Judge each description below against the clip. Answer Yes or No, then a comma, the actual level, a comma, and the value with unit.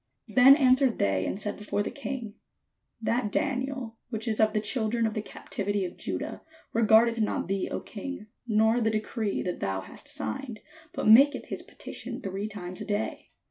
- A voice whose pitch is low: No, high, 220 Hz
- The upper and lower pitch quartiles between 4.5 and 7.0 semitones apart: No, average, 3.3 semitones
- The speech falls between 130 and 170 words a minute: No, average, 180 wpm